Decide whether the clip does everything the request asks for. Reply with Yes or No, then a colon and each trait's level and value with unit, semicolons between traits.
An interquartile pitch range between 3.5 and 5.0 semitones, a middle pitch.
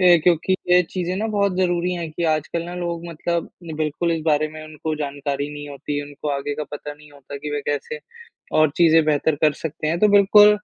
No: average, 3.1 semitones; medium, 160 Hz